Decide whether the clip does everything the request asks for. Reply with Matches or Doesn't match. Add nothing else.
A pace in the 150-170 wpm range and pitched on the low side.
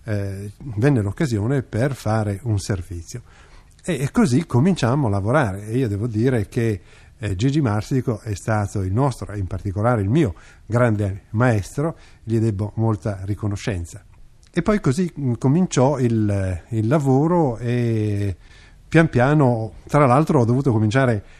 Doesn't match